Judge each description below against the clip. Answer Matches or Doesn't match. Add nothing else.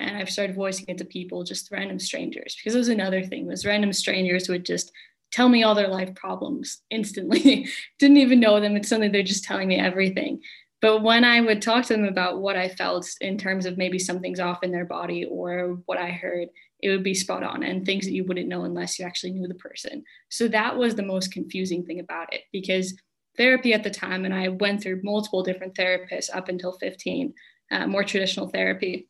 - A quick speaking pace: Matches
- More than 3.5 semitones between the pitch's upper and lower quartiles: Doesn't match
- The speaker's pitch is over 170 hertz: Matches